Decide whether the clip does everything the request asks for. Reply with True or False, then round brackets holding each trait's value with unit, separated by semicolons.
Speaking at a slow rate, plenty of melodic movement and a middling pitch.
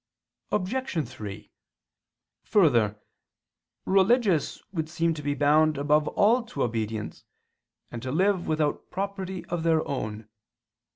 True (115 wpm; 6.4 semitones; 155 Hz)